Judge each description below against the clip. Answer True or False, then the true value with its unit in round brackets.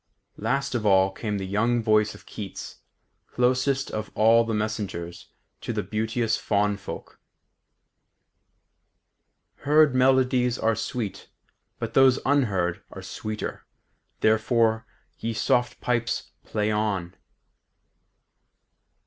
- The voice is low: True (110 Hz)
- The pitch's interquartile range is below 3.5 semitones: True (2.8 semitones)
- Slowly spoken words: True (105 wpm)